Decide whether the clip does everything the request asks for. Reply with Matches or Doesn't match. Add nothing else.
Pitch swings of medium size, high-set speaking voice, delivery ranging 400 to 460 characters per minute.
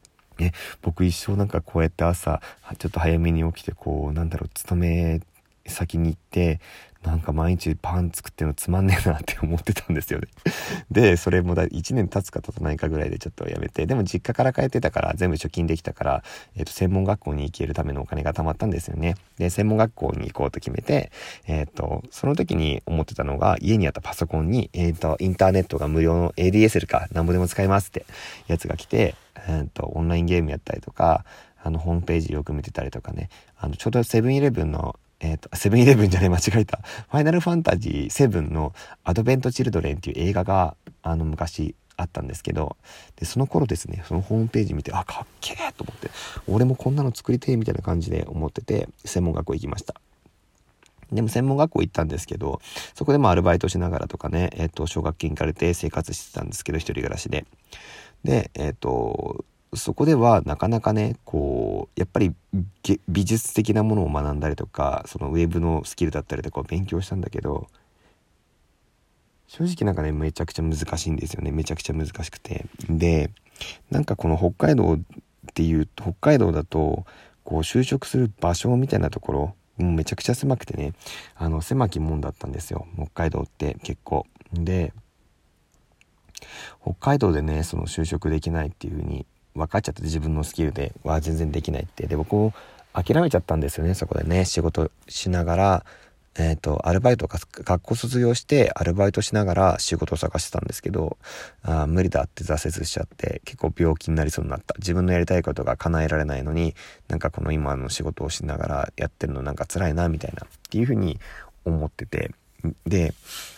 Doesn't match